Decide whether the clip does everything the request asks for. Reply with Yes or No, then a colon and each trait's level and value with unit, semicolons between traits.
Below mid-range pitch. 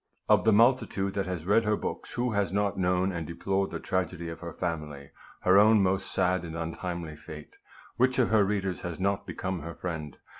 Yes: very low, 95 Hz